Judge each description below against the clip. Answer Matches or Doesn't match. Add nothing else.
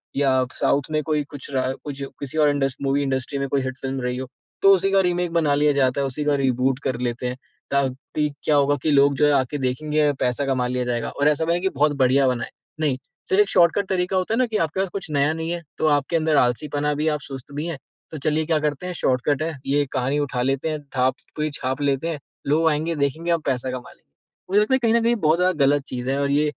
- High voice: Doesn't match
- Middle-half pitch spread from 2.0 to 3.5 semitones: Matches